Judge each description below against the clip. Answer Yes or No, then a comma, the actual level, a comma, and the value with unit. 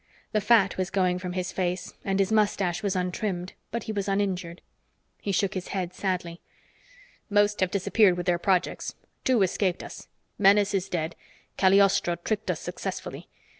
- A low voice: No, high, 190 Hz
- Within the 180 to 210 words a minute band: No, average, 165 wpm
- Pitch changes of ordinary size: No, narrow, 2.1 semitones